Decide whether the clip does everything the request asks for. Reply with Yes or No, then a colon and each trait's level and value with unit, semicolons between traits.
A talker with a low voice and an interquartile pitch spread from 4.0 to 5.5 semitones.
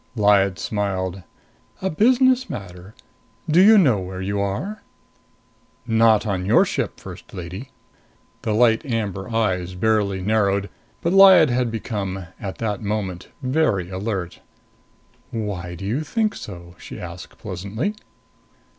Yes: low, 105 Hz; average, 4.5 semitones